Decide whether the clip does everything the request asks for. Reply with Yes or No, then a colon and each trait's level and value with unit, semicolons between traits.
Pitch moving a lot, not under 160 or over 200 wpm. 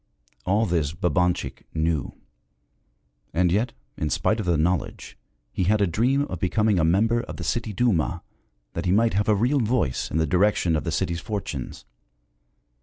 No: average, 4.7 semitones; average, 175 wpm